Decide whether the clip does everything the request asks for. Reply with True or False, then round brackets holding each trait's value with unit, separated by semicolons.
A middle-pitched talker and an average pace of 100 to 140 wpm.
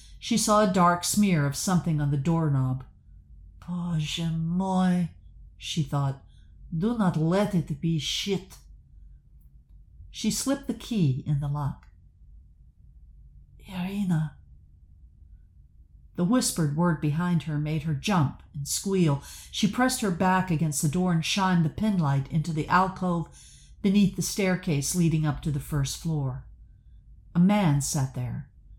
True (155 Hz; 135 wpm)